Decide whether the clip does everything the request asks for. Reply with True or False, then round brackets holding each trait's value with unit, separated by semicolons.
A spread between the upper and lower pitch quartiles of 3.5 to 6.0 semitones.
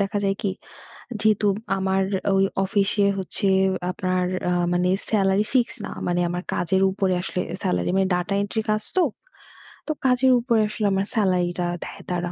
False (2.8 semitones)